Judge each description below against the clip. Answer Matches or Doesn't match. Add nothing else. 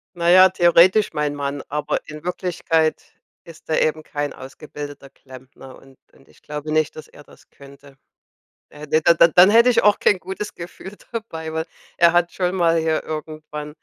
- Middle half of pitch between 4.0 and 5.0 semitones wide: Doesn't match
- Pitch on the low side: Doesn't match